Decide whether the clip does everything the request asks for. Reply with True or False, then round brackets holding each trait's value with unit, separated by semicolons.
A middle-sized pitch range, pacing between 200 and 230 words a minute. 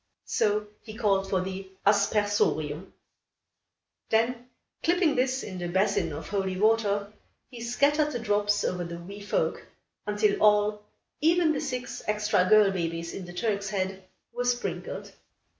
False (3.5 semitones; 140 wpm)